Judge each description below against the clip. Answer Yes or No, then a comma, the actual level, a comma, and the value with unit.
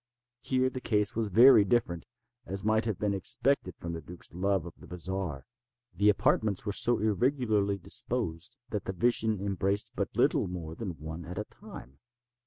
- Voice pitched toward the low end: Yes, low, 100 Hz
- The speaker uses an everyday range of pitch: Yes, average, 3.8 semitones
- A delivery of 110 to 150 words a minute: No, average, 175 wpm